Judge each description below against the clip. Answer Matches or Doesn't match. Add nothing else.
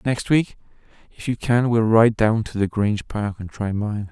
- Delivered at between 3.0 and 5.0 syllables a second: Matches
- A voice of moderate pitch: Doesn't match